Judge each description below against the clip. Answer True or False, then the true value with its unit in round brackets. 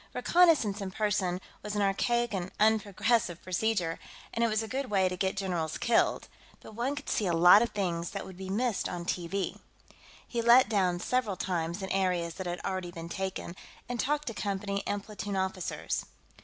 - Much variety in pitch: False (3.6 semitones)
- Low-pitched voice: False (195 Hz)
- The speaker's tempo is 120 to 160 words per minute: False (190 wpm)